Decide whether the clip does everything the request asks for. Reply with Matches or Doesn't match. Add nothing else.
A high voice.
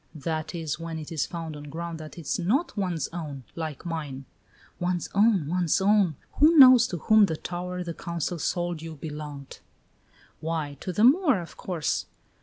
Doesn't match